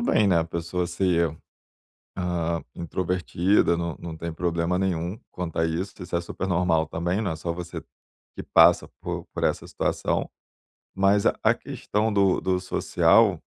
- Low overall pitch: Yes, very low, 90 Hz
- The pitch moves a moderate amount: No, narrow, 2.0 semitones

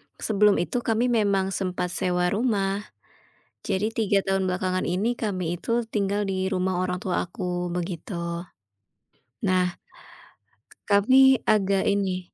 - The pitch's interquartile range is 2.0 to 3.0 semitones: Yes, narrow, 2.5 semitones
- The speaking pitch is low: No, high, 195 Hz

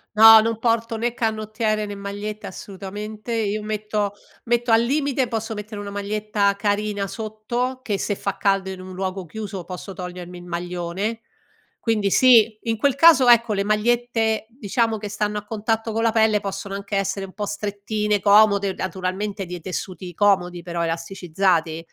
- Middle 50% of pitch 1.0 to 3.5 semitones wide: Yes, narrow, 2.4 semitones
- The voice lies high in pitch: Yes, high, 210 Hz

